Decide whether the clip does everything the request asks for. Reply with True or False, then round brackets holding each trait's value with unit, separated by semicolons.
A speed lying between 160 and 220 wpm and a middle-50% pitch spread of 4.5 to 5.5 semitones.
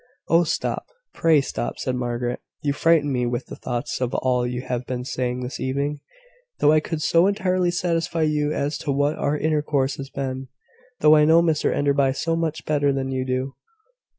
False (190 wpm; 3.2 semitones)